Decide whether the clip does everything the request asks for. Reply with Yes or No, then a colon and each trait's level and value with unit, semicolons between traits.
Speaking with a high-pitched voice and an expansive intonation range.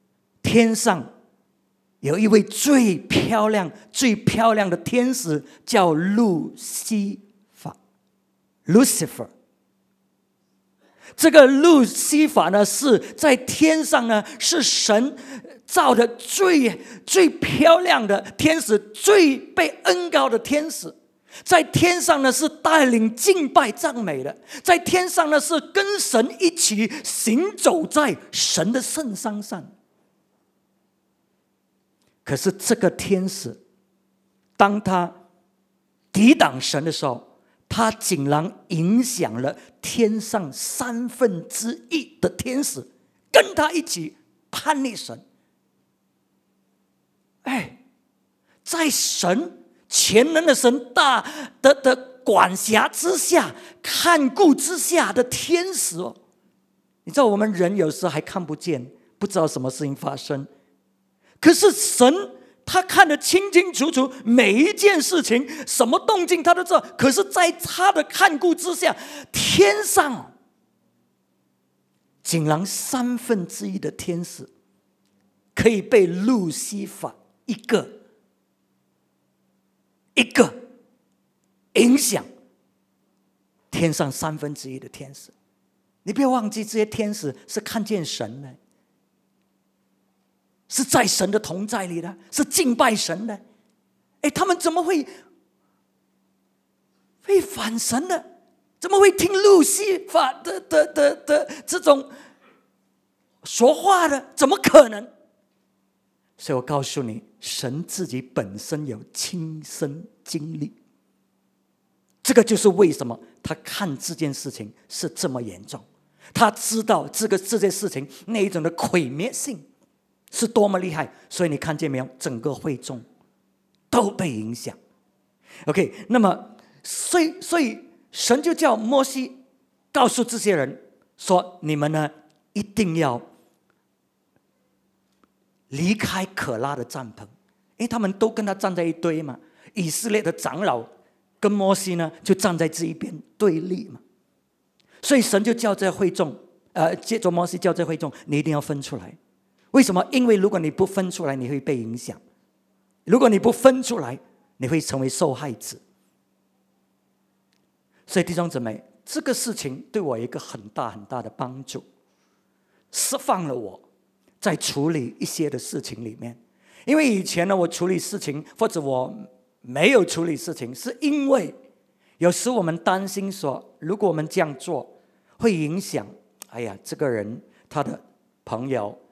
Yes: high, 210 Hz; wide, 9.0 semitones